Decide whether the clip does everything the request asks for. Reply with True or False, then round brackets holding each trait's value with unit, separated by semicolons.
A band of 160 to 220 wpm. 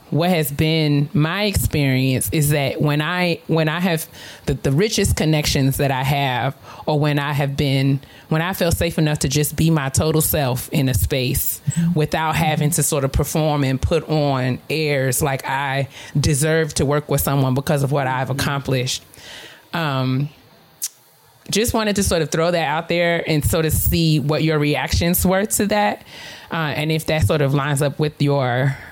True (185 wpm)